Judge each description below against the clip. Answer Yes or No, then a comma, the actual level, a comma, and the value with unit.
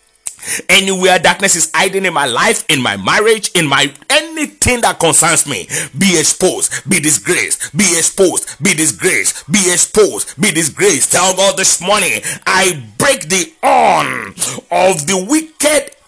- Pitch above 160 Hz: Yes, medium, 185 Hz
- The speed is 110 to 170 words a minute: Yes, average, 145 wpm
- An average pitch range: Yes, average, 4.5 semitones